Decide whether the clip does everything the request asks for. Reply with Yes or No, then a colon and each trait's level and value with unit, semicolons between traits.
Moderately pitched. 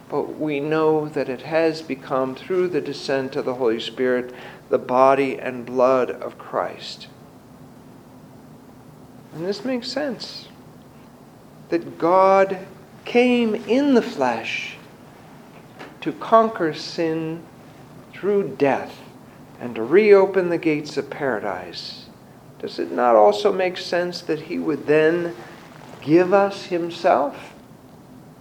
Yes: medium, 155 Hz